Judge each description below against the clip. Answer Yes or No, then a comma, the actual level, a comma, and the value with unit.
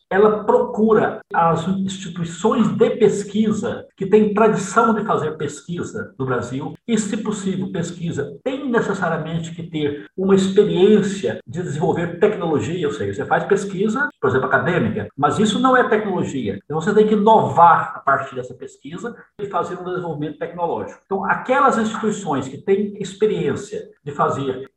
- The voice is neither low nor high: No, high, 200 Hz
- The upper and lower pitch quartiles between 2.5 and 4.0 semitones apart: No, average, 4.6 semitones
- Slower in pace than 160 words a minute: Yes, average, 150 wpm